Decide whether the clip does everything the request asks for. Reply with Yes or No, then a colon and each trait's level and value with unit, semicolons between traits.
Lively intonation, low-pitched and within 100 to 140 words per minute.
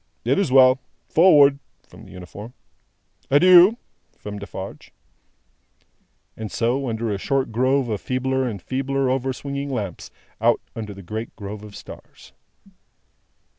No: average, 4.3 semitones; low, 130 Hz; slow, 135 wpm